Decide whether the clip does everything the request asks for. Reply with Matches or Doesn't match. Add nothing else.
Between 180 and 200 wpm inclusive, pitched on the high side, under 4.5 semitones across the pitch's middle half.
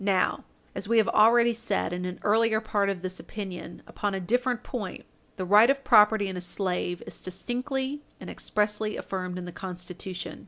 Matches